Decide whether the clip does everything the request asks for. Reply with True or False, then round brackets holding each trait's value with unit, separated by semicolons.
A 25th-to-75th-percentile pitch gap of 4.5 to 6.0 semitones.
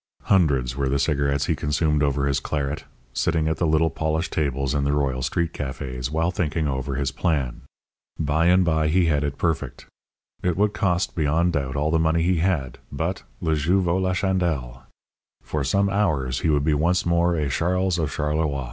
False (3.5 semitones)